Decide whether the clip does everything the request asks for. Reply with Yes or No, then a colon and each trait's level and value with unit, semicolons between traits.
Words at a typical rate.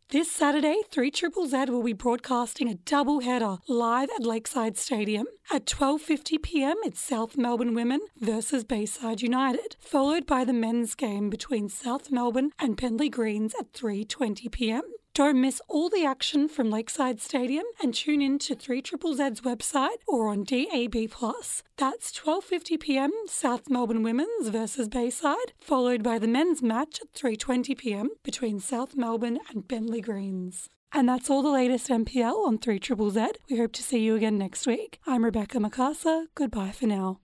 Yes: average, 160 wpm